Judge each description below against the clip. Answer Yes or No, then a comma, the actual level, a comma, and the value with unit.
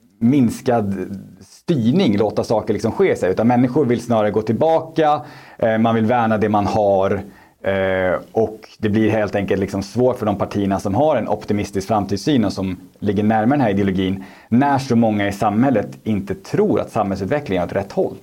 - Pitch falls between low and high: No, low, 105 Hz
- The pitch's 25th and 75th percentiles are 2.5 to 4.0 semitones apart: Yes, average, 3.1 semitones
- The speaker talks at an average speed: Yes, average, 175 wpm